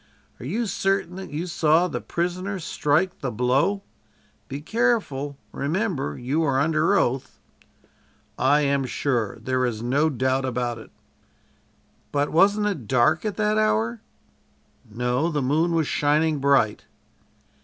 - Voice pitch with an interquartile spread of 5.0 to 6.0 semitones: Yes, wide, 5.4 semitones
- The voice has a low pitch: No, medium, 145 Hz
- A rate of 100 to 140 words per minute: Yes, slow, 135 wpm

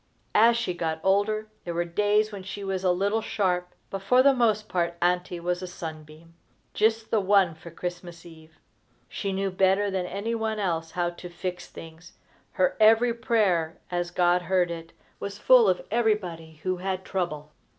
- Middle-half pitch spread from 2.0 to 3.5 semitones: Yes, average, 3.2 semitones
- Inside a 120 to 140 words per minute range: No, average, 180 wpm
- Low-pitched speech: No, medium, 185 Hz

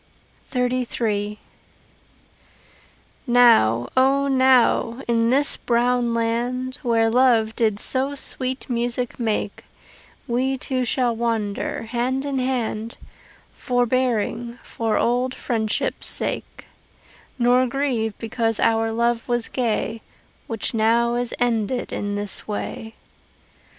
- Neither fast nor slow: No, slow, 105 wpm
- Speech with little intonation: Yes, narrow, 2.0 semitones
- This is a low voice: No, high, 235 Hz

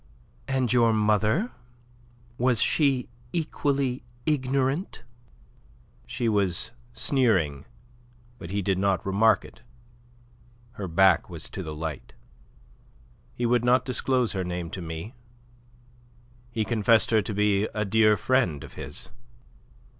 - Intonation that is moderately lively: Yes, average, 4.8 semitones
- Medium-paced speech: No, slow, 120 wpm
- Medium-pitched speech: No, low, 110 Hz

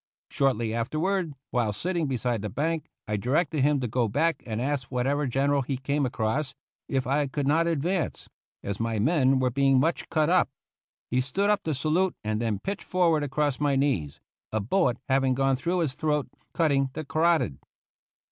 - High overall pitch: No, medium, 140 Hz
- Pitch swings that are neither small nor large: Yes, average, 3.9 semitones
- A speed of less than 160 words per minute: No, average, 185 wpm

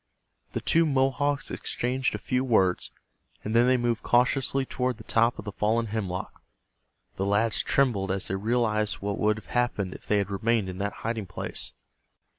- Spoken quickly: No, average, 180 wpm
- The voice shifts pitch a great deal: No, average, 3.6 semitones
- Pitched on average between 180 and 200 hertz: No, low, 115 Hz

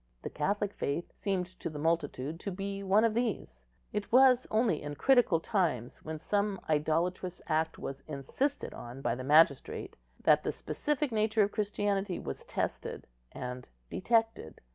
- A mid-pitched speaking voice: Yes, medium, 180 Hz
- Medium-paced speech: Yes, average, 155 wpm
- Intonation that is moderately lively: No, wide, 6.1 semitones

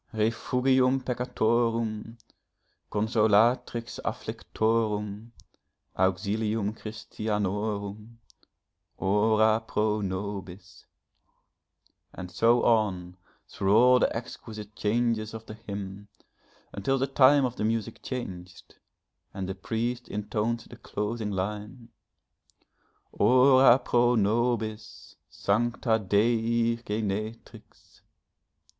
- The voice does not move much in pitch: Yes, narrow, 2.3 semitones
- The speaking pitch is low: Yes, low, 110 Hz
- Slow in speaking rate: Yes, slow, 85 wpm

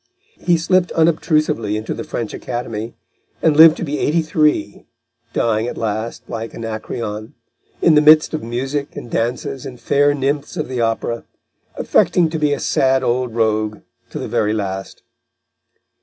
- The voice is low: Yes, low, 125 Hz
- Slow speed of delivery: No, average, 155 wpm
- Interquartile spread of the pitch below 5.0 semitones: No, average, 5.3 semitones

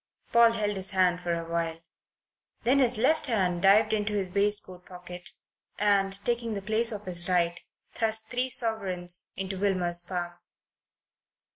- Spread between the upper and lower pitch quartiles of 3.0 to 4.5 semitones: Yes, average, 3.7 semitones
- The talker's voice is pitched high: Yes, high, 195 Hz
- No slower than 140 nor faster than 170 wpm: Yes, average, 150 wpm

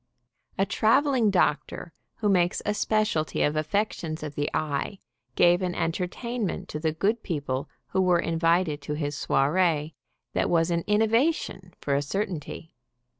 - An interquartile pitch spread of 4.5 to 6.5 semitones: Yes, average, 5.0 semitones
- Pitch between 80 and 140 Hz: No, medium, 175 Hz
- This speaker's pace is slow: No, average, 155 wpm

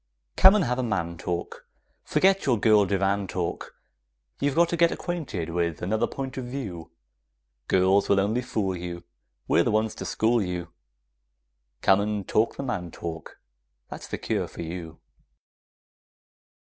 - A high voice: No, low, 100 Hz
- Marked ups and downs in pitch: Yes, wide, 6.0 semitones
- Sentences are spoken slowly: No, average, 155 wpm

